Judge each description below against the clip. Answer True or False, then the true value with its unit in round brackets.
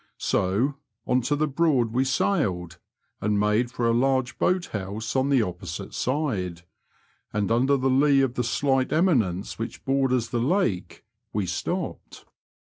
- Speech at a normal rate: True (150 wpm)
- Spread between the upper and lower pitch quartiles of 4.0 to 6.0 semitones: True (4.5 semitones)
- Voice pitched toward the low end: True (125 Hz)